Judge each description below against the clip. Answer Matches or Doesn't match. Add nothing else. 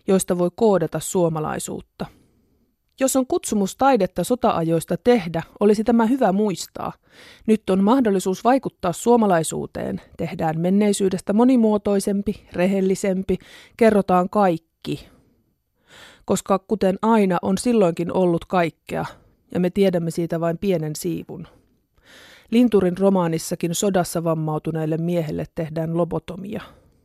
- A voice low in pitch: Doesn't match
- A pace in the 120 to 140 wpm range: Doesn't match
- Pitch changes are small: Doesn't match